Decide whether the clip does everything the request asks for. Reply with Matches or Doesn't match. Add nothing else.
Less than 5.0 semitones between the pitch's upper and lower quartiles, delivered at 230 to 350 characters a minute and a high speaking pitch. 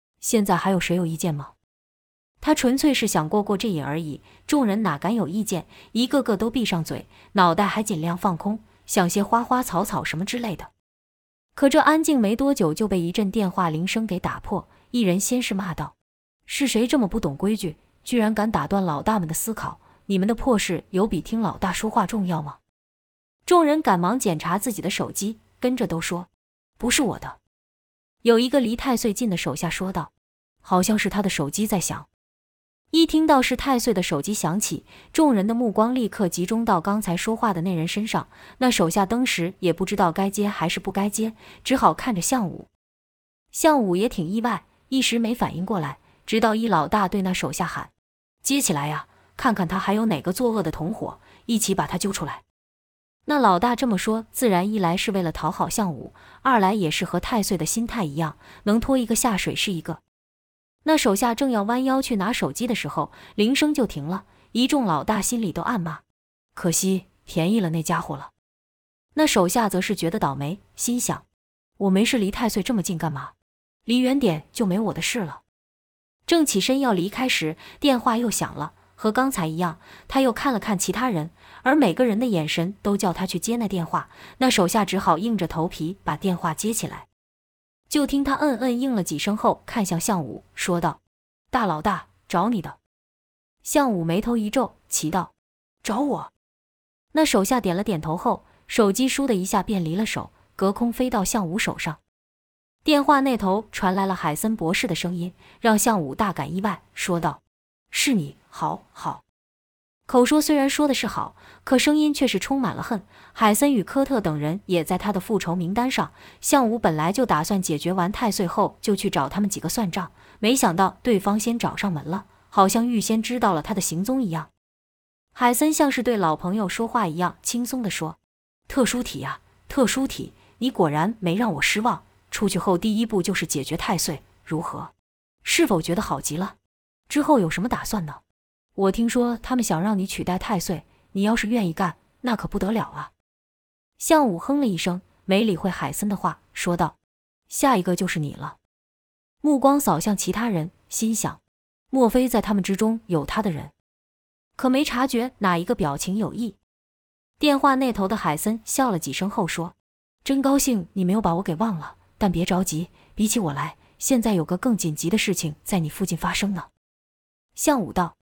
Doesn't match